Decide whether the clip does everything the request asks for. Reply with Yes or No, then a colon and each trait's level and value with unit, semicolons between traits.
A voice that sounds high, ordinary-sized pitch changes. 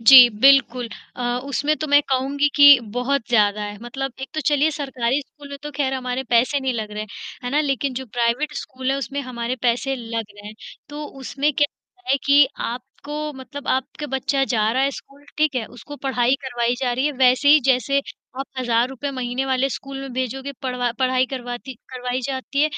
No: very high, 265 Hz; narrow, 2.3 semitones